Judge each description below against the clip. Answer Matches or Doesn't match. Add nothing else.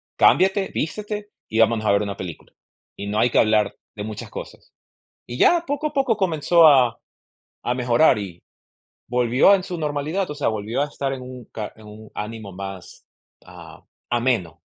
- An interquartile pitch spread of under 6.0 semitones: Doesn't match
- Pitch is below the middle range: Matches